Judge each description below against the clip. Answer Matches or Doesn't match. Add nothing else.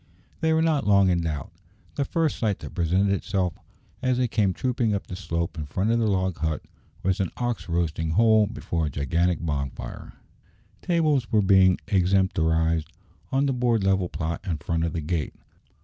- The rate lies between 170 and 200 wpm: Matches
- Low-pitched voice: Matches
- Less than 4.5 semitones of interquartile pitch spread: Doesn't match